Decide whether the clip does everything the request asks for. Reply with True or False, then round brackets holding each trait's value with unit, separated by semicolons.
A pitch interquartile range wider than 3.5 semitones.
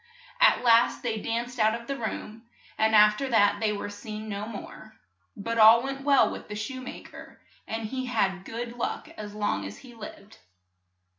False (2.4 semitones)